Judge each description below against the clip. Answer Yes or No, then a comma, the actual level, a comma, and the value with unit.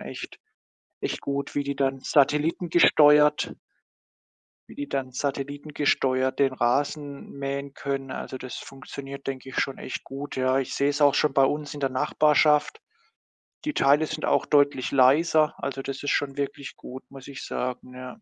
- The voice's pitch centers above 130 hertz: Yes, medium, 140 Hz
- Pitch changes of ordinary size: No, narrow, 1.5 semitones